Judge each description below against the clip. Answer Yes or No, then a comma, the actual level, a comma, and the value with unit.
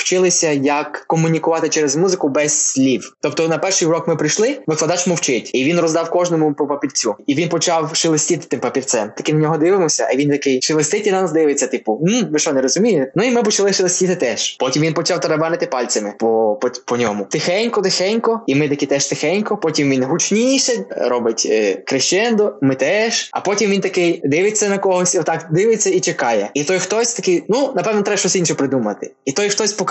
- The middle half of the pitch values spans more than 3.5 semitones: Yes, average, 4.3 semitones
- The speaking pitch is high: No, medium, 165 Hz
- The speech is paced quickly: Yes, fast, 190 wpm